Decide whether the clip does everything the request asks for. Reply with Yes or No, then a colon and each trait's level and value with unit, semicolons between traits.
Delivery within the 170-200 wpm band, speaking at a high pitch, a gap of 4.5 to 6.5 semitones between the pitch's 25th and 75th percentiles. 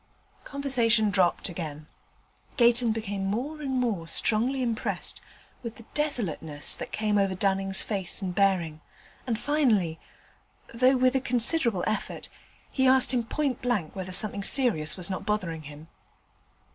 No: average, 140 wpm; high, 215 Hz; average, 5.2 semitones